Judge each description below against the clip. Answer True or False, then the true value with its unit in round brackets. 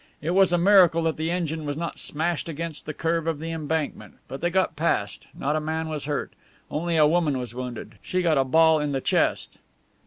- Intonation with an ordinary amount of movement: False (2.2 semitones)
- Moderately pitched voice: True (160 Hz)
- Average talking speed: False (220 wpm)